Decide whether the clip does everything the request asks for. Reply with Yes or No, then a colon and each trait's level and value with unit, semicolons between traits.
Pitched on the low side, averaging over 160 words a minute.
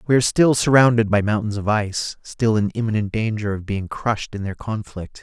Yes: low, 110 Hz; fast, 205 wpm